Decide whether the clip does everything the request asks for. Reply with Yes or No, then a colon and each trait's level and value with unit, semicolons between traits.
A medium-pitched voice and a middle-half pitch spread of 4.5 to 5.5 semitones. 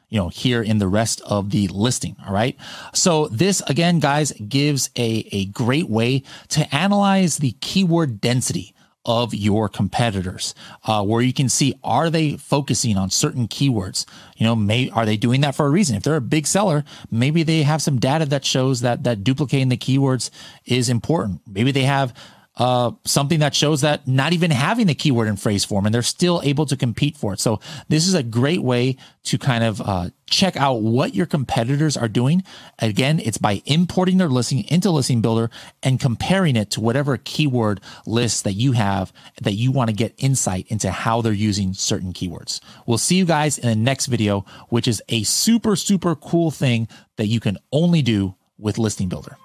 No: low, 130 Hz; average, 5.2 semitones